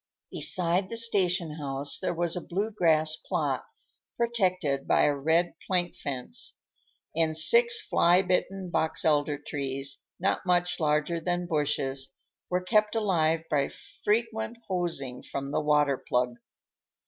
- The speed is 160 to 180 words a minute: No, slow, 135 wpm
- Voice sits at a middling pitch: Yes, medium, 170 Hz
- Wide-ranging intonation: No, average, 4.0 semitones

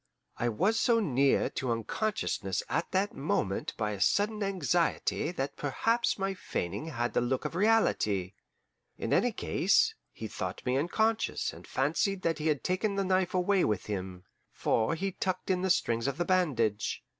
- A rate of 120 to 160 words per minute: No, average, 170 wpm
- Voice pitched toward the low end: No, medium, 165 Hz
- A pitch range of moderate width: No, wide, 8.6 semitones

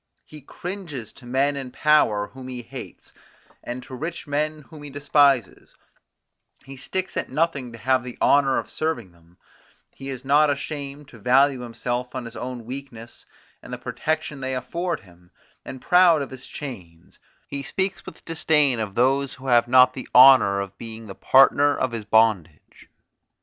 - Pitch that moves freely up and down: No, average, 3.5 semitones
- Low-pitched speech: Yes, low, 130 Hz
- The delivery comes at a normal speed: Yes, average, 170 wpm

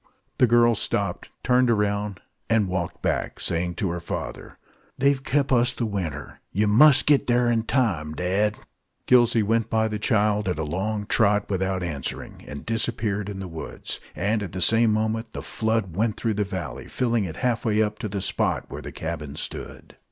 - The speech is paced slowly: No, average, 190 wpm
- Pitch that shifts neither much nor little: Yes, average, 3.7 semitones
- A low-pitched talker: Yes, low, 105 Hz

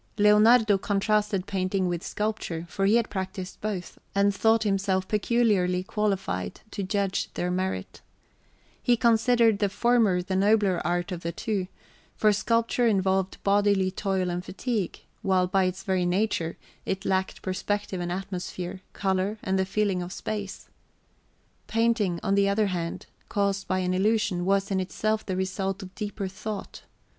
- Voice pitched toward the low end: No, high, 195 Hz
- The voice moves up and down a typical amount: No, narrow, 2.3 semitones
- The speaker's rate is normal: Yes, average, 150 wpm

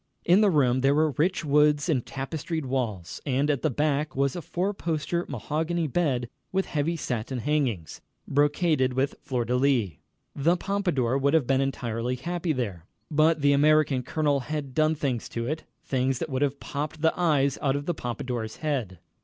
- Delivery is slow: No, average, 180 wpm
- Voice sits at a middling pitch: Yes, medium, 145 Hz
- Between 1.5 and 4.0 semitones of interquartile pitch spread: Yes, average, 3.5 semitones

